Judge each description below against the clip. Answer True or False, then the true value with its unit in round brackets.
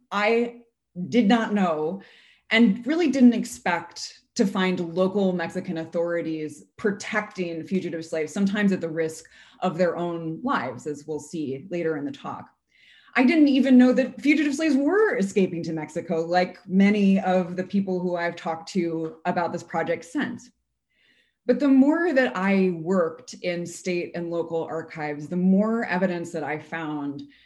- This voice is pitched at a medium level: True (180 Hz)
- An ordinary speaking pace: True (155 wpm)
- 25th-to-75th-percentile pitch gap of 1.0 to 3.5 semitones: False (4.6 semitones)